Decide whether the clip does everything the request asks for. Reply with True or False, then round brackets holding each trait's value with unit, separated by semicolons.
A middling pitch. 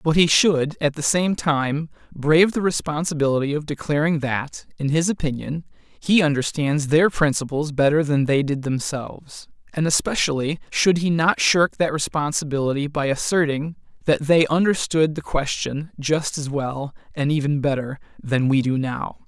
True (150 Hz)